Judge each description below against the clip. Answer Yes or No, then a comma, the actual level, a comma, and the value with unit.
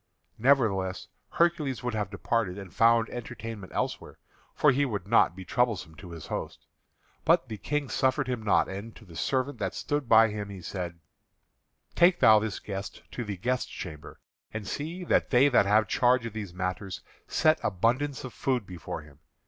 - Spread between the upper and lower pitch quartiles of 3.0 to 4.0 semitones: No, average, 5.0 semitones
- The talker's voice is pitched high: No, low, 110 Hz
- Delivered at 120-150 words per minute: No, average, 175 wpm